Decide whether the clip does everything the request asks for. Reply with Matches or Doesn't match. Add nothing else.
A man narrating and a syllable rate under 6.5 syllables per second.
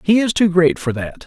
Matches